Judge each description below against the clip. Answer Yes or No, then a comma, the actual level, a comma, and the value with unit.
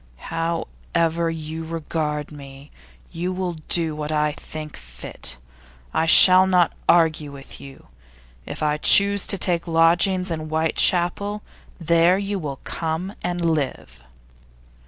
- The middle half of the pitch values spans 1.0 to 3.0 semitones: Yes, narrow, 2.6 semitones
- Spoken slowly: Yes, slow, 125 wpm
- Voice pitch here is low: No, medium, 165 Hz